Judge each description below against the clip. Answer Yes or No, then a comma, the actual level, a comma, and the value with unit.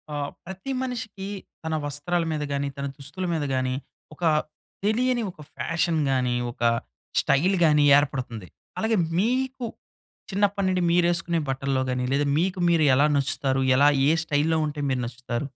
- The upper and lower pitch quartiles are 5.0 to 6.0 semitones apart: Yes, wide, 5.5 semitones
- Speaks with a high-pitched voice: No, medium, 155 Hz